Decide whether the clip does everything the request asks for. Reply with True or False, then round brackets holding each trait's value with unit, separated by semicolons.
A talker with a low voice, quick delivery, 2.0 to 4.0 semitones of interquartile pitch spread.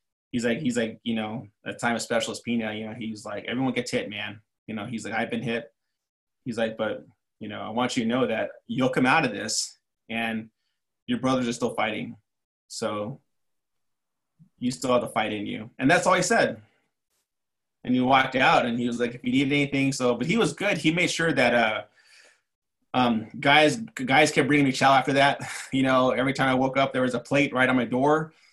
True (125 Hz; 225 wpm; 3.5 semitones)